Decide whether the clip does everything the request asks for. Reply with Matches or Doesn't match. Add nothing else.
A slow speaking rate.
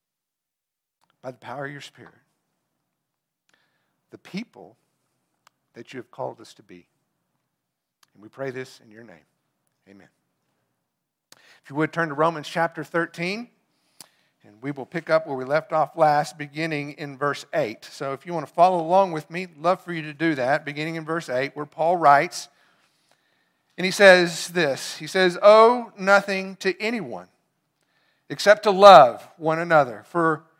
Doesn't match